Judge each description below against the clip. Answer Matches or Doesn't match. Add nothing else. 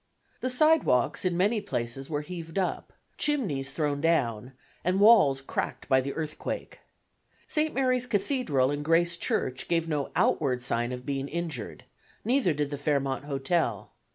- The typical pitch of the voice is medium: Matches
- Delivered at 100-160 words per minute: Matches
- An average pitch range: Doesn't match